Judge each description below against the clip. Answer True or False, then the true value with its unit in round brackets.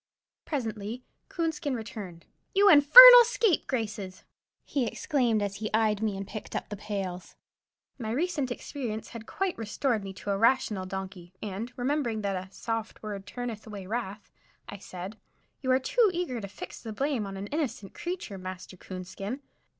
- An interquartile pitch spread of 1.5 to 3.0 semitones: False (5.3 semitones)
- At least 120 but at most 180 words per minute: True (160 wpm)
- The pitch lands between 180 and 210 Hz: False (220 Hz)